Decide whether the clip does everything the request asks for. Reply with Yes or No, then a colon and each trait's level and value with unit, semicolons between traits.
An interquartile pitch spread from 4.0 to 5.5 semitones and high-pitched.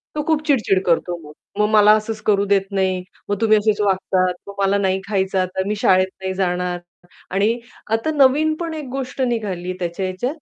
No: average, 3.3 semitones; high, 200 Hz